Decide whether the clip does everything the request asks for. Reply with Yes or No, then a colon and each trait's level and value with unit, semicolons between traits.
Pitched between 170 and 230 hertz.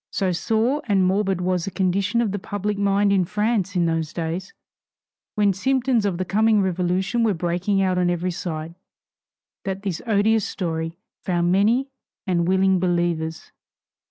Yes: high, 190 Hz